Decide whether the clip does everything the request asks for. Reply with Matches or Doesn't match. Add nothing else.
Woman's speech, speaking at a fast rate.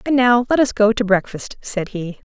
Matches